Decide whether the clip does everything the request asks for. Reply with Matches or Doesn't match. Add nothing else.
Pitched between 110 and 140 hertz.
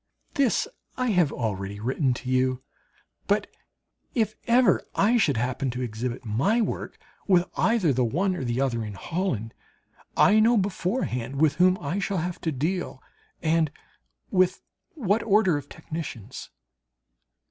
Doesn't match